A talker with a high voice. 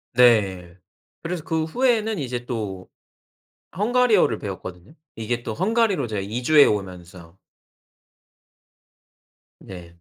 No: low, 120 Hz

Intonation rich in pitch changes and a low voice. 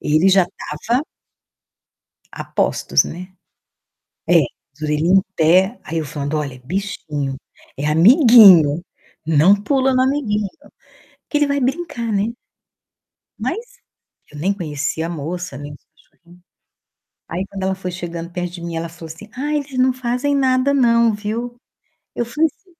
No: wide, 7.3 semitones; high, 190 Hz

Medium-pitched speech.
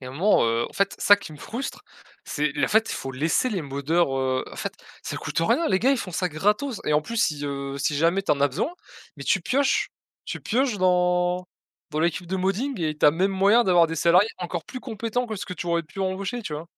Yes: medium, 180 Hz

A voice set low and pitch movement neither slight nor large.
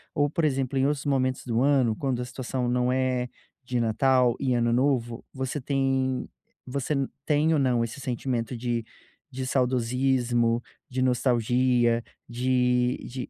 No: low, 125 Hz; narrow, 1.6 semitones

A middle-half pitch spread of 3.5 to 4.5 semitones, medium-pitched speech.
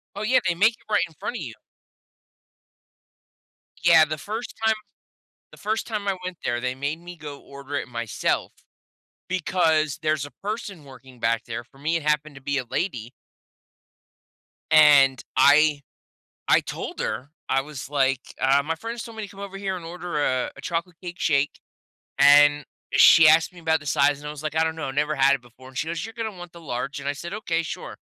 Yes: average, 4.2 semitones; medium, 155 Hz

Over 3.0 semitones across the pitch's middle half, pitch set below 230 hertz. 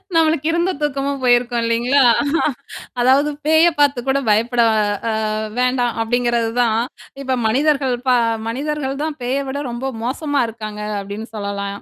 No: average, 3.5 semitones; very high, 255 Hz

